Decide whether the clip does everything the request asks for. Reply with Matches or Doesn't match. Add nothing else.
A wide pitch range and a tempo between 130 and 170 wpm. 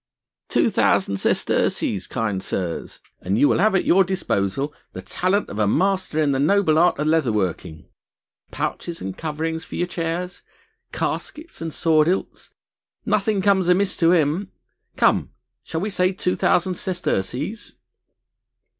Matches